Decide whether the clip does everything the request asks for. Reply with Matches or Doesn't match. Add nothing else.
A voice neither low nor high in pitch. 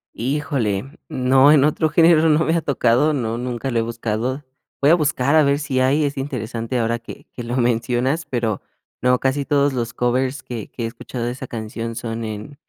Doesn't match